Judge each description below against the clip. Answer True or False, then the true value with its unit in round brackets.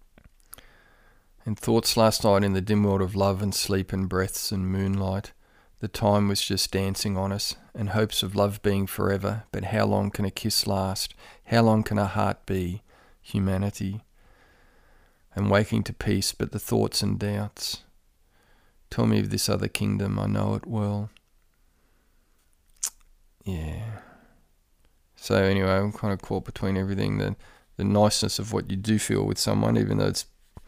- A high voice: False (100 Hz)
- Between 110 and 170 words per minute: True (165 wpm)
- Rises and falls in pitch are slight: True (1.8 semitones)